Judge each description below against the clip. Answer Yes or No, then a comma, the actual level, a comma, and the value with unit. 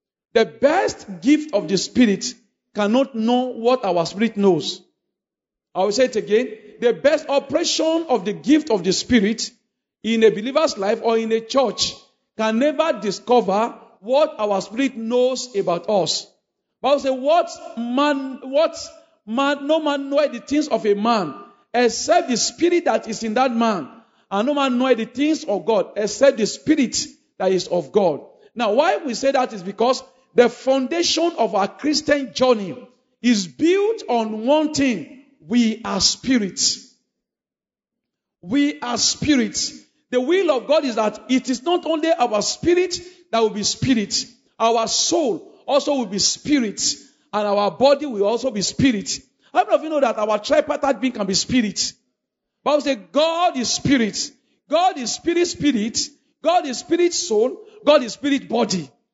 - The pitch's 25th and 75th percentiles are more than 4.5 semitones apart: Yes, average, 5.0 semitones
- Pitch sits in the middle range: No, very high, 255 Hz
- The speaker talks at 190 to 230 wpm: No, average, 170 wpm